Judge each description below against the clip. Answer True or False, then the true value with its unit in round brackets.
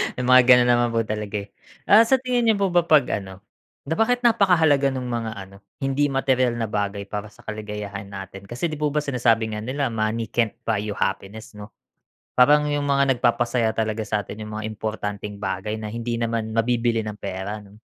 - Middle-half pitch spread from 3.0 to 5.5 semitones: True (4.4 semitones)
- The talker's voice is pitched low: True (115 Hz)